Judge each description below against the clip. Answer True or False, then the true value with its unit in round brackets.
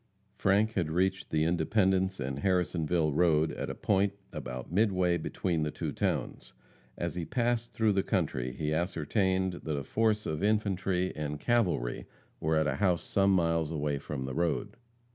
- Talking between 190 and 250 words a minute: False (165 wpm)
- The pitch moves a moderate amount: True (4.1 semitones)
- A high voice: False (90 Hz)